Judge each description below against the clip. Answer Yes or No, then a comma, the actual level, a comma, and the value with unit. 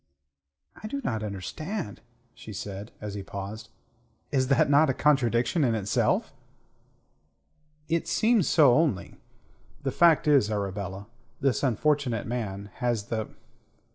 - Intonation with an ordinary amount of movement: No, wide, 6.3 semitones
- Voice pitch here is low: Yes, low, 120 Hz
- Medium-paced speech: No, slow, 125 wpm